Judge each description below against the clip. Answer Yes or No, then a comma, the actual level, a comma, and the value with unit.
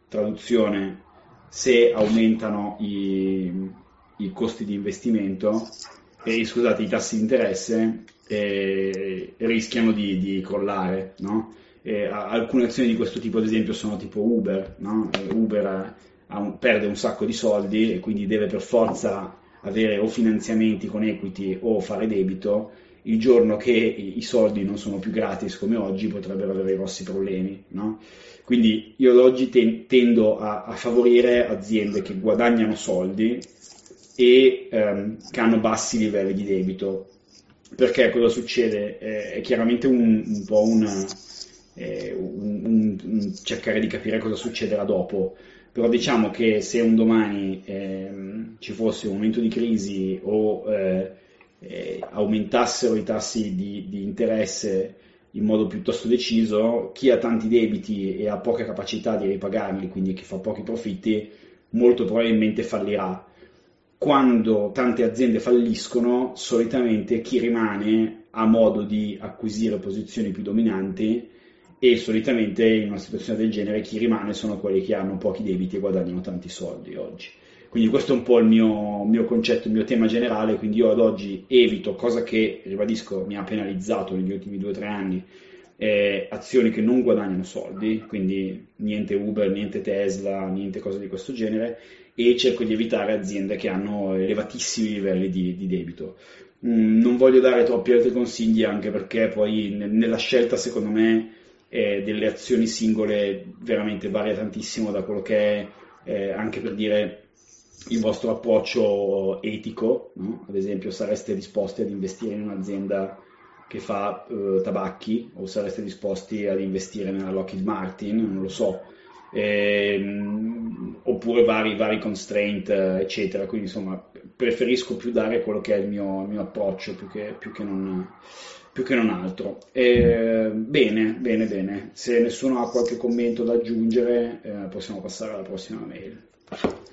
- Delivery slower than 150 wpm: No, average, 155 wpm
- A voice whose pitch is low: Yes, low, 110 Hz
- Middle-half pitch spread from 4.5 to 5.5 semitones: No, average, 2.7 semitones